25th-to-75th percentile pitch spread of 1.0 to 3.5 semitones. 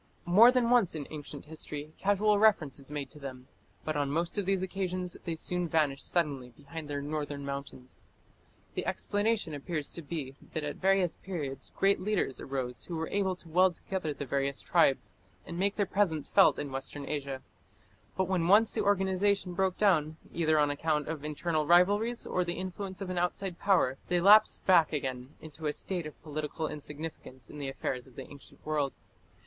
No: average, 4.6 semitones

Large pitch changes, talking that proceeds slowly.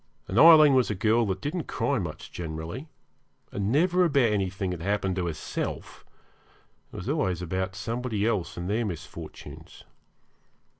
No: wide, 5.8 semitones; average, 150 wpm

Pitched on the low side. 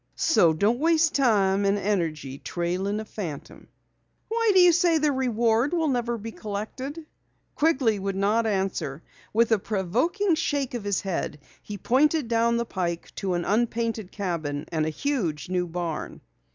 No: high, 215 Hz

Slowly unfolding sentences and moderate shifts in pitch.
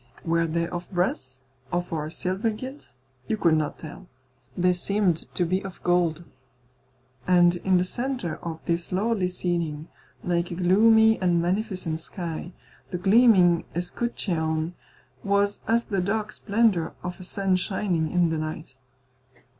No: average, 145 wpm; average, 3.0 semitones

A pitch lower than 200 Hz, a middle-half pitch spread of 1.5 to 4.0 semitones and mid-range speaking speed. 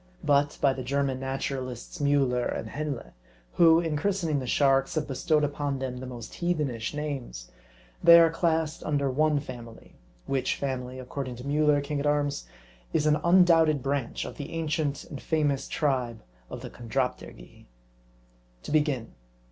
Yes: medium, 140 Hz; average, 2.8 semitones; average, 160 wpm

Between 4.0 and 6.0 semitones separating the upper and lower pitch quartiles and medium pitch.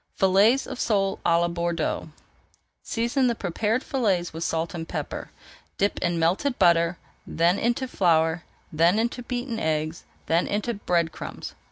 Yes: wide, 5.5 semitones; medium, 180 Hz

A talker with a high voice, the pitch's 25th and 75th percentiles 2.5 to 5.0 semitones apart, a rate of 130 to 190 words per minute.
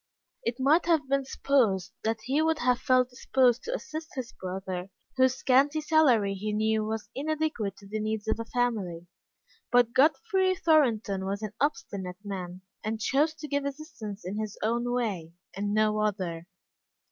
No: high, 230 Hz; wide, 5.6 semitones; average, 165 wpm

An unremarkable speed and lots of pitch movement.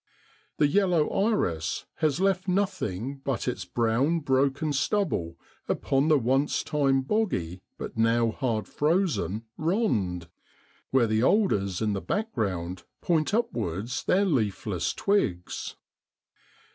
No: slow, 120 wpm; wide, 8.3 semitones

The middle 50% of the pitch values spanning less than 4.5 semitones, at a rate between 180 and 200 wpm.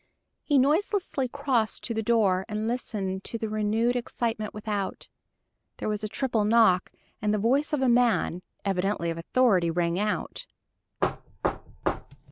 No: average, 3.7 semitones; average, 140 wpm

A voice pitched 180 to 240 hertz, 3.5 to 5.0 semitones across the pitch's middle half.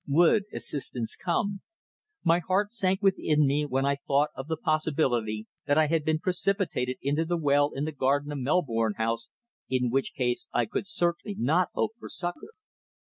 No: medium, 150 Hz; average, 4.7 semitones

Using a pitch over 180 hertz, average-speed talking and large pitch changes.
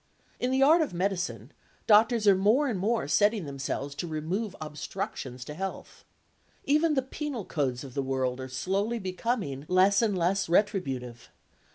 Yes: high, 190 Hz; average, 160 wpm; wide, 7.9 semitones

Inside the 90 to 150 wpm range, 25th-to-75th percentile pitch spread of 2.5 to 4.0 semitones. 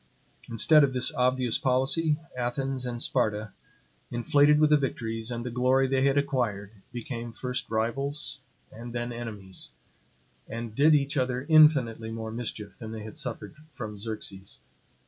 Yes: average, 145 wpm; average, 3.2 semitones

